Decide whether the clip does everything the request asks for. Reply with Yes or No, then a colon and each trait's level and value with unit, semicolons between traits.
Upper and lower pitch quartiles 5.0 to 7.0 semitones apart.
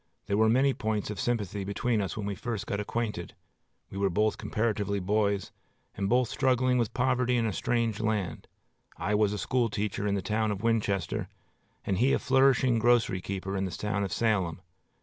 No: average, 3.0 semitones